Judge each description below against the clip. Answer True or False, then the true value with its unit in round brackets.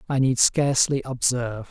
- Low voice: True (130 Hz)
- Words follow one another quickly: False (140 wpm)